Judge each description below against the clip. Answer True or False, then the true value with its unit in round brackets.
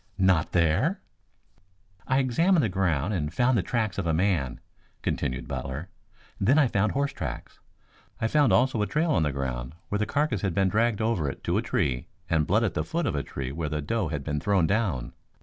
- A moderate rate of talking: False (210 wpm)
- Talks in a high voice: False (95 Hz)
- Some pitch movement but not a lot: False (7.3 semitones)